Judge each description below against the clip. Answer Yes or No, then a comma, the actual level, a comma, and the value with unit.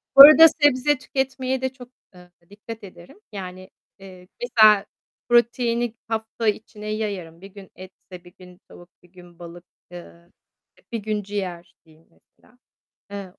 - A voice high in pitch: Yes, high, 205 Hz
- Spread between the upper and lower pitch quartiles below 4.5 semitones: No, average, 4.8 semitones